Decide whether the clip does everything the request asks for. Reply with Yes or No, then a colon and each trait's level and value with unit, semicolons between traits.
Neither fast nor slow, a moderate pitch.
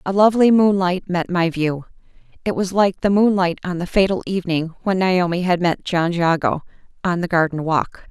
Yes: average, 185 wpm; medium, 180 Hz